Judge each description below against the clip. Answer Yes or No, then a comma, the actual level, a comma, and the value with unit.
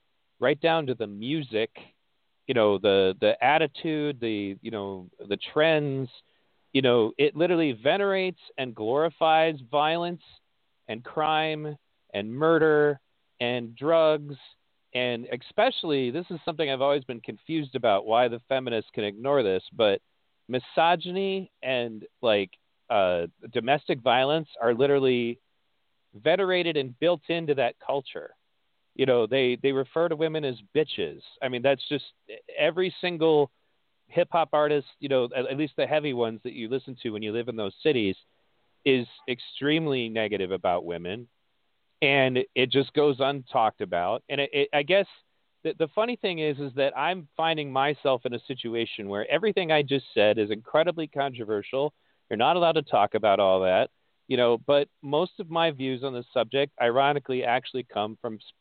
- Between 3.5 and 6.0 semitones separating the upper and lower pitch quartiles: Yes, average, 4.6 semitones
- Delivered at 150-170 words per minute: Yes, average, 160 wpm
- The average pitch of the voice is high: No, medium, 140 Hz